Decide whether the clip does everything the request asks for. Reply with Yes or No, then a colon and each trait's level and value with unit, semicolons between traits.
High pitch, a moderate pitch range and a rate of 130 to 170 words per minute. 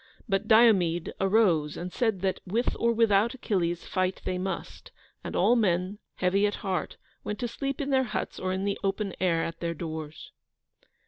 No: high, 195 Hz; average, 3.8 semitones; average, 180 wpm